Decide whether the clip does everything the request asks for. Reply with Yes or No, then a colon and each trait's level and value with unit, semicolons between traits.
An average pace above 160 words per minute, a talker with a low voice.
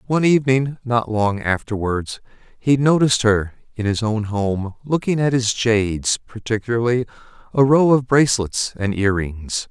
No: average, 150 wpm; low, 115 Hz